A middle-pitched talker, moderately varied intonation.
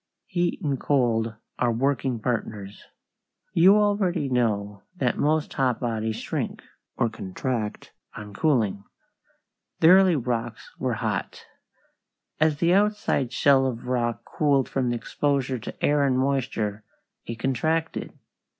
No: low, 130 Hz; average, 4.5 semitones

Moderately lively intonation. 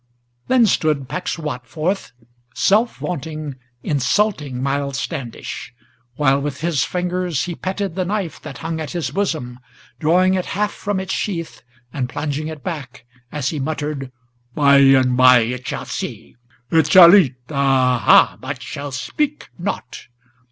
Yes: average, 5.0 semitones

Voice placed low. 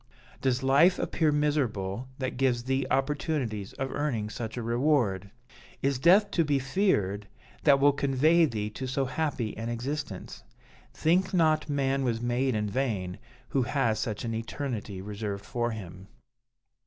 Yes: low, 130 Hz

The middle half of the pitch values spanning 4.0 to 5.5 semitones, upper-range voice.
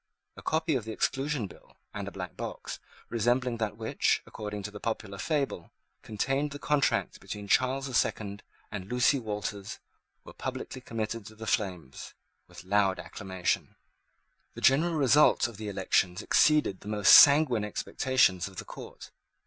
No: average, 4.8 semitones; low, 110 Hz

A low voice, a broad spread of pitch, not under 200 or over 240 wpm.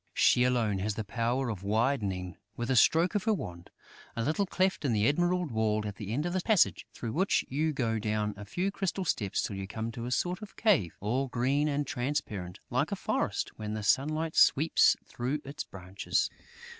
Yes: low, 125 Hz; wide, 6.7 semitones; fast, 205 wpm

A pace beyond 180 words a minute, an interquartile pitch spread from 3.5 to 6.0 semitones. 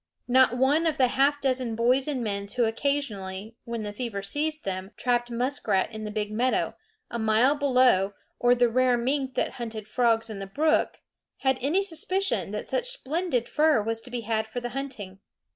Yes: average, 190 wpm; average, 3.9 semitones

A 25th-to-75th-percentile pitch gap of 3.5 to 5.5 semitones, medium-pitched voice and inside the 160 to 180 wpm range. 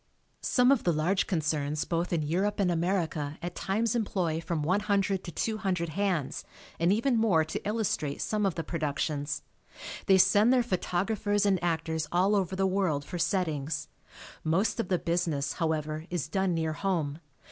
Yes: average, 4.0 semitones; medium, 175 Hz; average, 170 wpm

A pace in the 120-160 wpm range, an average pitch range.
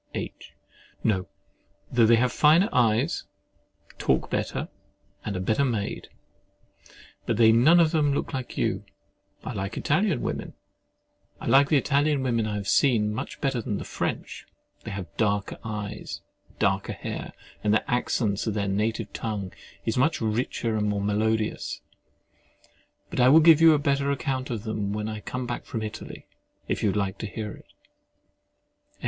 Yes: average, 155 wpm; average, 4.6 semitones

